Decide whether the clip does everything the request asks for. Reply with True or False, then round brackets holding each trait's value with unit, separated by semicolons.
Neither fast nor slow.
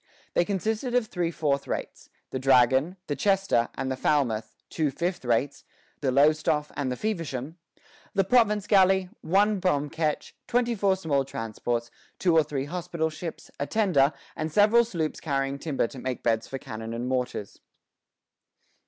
True (160 wpm)